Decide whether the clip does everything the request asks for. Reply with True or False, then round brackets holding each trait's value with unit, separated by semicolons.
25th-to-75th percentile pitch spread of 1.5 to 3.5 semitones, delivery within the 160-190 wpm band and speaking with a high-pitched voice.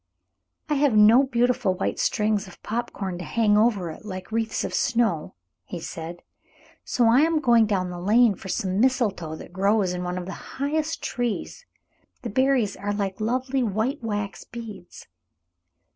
False (4.4 semitones; 175 wpm; 215 Hz)